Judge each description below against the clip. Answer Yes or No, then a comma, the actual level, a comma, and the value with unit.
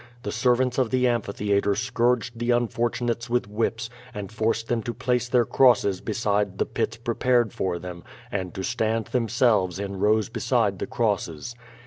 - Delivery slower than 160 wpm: No, average, 165 wpm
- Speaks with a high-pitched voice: No, low, 115 Hz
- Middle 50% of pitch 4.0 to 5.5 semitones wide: No, average, 3.0 semitones